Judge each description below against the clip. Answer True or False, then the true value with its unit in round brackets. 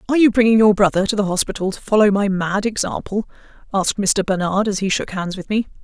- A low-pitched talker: False (200 Hz)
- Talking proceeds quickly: True (225 wpm)